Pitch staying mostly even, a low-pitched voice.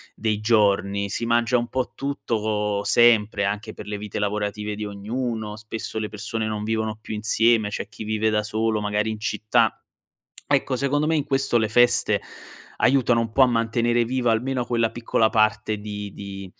Yes: narrow, 2.1 semitones; low, 110 Hz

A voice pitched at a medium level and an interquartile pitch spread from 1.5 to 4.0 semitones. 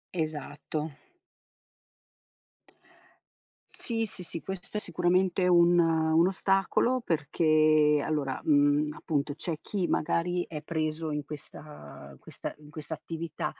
Yes: medium, 160 Hz; average, 2.7 semitones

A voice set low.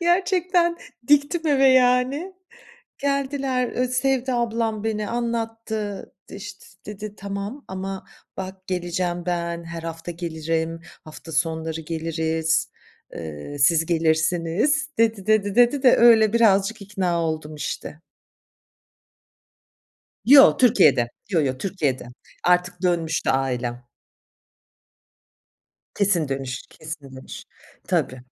No: high, 190 Hz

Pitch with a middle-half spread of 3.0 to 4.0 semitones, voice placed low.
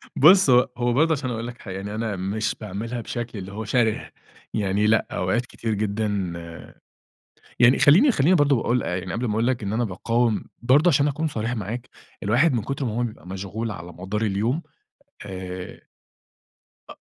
Yes: average, 3.7 semitones; low, 115 Hz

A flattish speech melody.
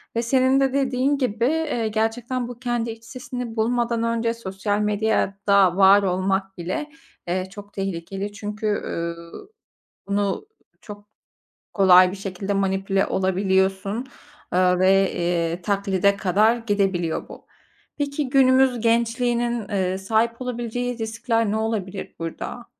No: average, 3.7 semitones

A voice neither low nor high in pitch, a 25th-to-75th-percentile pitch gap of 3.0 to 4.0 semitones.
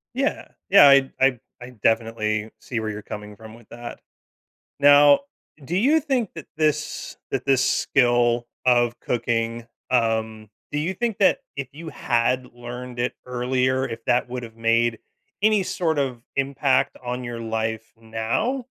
No: low, 125 Hz; average, 3.7 semitones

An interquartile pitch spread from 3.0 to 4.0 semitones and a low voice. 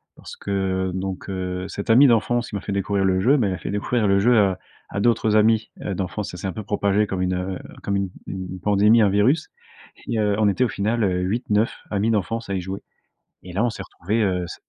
No: narrow, 2.6 semitones; low, 100 Hz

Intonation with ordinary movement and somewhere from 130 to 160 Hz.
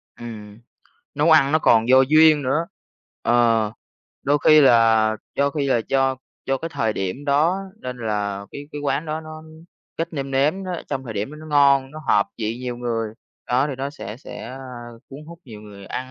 Yes: average, 4.7 semitones; low, 135 Hz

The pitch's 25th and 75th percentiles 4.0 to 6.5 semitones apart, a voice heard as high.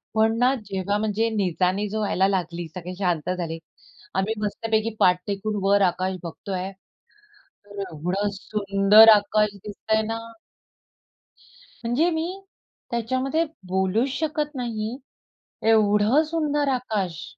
No: average, 3.3 semitones; high, 210 Hz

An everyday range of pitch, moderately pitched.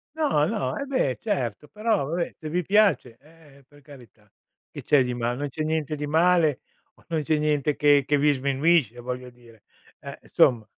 Yes: average, 4.4 semitones; medium, 145 Hz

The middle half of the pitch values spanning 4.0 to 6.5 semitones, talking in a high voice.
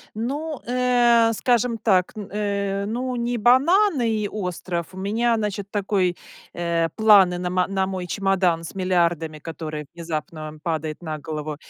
Yes: average, 5.1 semitones; high, 195 Hz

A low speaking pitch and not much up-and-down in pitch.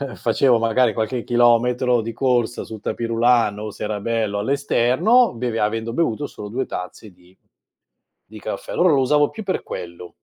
No: low, 115 Hz; average, 3.0 semitones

